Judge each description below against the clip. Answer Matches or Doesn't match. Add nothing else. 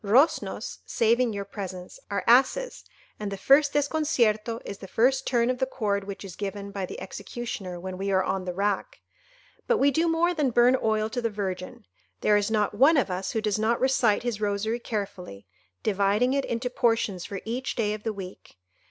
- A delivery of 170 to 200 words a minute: Matches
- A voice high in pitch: Matches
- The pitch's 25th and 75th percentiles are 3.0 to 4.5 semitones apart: Matches